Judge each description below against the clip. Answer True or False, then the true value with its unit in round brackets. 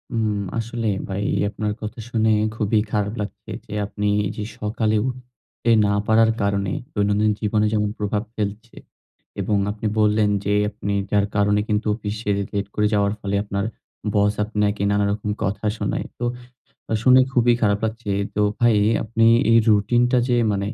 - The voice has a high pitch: False (105 Hz)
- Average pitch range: False (1.5 semitones)